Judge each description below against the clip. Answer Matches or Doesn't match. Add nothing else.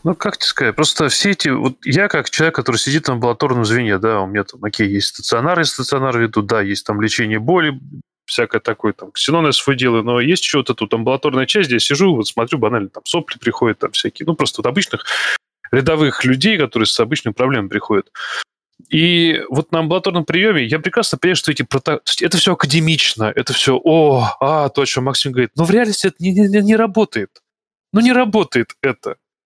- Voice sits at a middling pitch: Matches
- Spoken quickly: Matches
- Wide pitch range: Matches